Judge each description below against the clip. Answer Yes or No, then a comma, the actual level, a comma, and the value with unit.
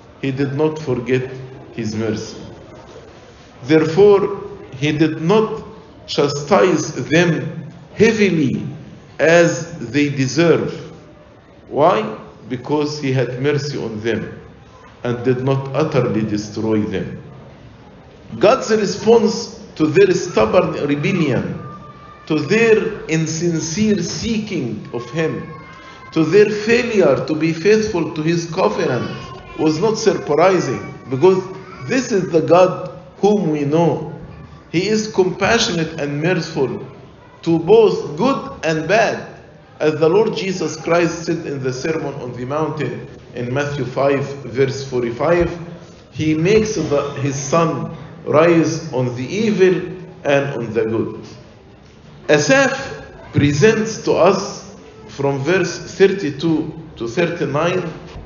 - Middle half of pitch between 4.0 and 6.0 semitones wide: Yes, average, 4.6 semitones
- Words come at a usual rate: No, slow, 115 wpm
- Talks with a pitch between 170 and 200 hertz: No, medium, 160 Hz